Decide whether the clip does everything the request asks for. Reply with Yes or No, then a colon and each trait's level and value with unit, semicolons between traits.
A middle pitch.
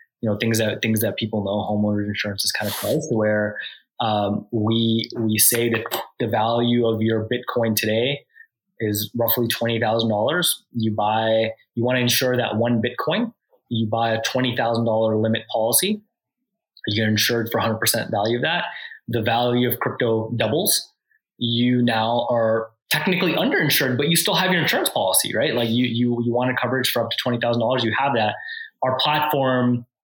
No: low, 115 Hz